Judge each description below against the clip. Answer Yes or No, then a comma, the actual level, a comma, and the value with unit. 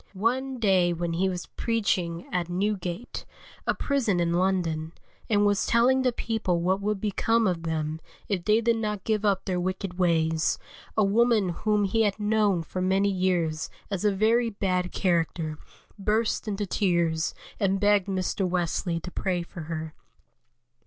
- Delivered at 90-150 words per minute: No, average, 160 wpm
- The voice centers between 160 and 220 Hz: Yes, high, 190 Hz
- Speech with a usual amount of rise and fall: Yes, average, 3.4 semitones